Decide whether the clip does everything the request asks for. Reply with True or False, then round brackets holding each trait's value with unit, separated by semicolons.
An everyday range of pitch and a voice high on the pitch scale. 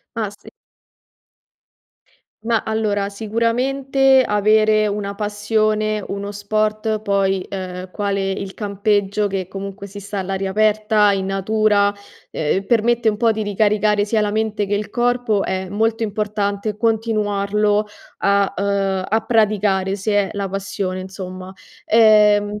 False (1.5 semitones; 205 Hz)